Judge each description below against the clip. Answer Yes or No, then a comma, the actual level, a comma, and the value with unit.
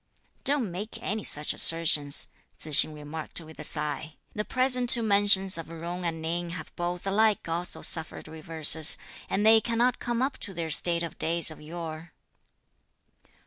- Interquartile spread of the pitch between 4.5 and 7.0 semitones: Yes, average, 4.8 semitones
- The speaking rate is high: No, average, 165 wpm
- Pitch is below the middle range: No, medium, 170 Hz